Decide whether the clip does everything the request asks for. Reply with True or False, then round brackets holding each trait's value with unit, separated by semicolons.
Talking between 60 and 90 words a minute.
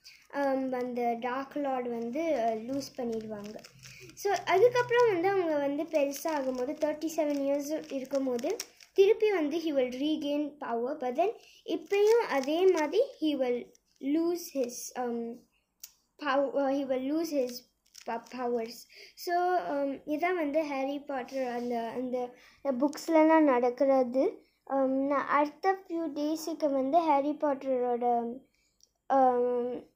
False (105 wpm)